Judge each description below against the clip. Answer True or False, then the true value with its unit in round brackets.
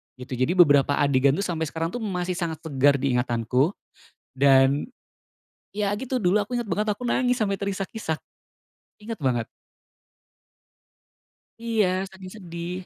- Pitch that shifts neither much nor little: False (6.7 semitones)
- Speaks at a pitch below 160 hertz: False (175 Hz)